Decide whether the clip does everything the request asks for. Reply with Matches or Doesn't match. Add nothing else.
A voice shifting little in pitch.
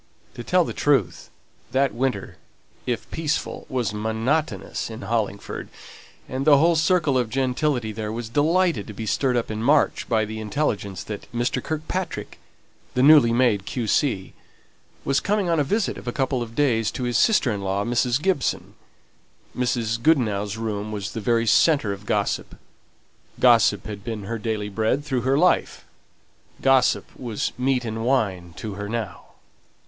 Doesn't match